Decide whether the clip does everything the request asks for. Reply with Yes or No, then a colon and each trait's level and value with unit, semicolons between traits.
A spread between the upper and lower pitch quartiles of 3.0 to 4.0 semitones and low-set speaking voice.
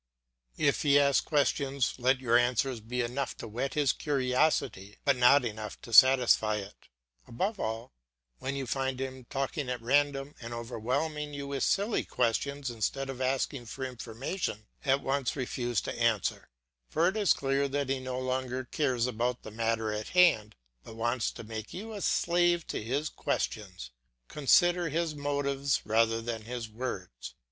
Yes: average, 3.3 semitones; low, 130 Hz